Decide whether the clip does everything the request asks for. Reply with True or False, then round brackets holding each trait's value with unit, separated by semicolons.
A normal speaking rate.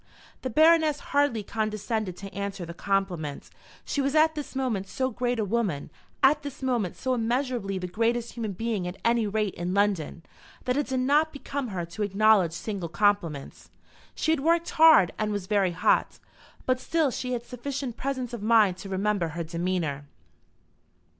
True (175 wpm)